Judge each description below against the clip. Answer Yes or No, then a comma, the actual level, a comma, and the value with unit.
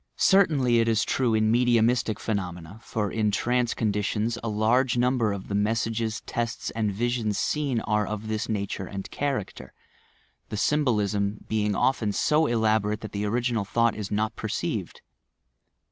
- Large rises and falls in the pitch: No, narrow, 2.4 semitones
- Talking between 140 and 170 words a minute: Yes, average, 155 wpm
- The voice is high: No, low, 110 Hz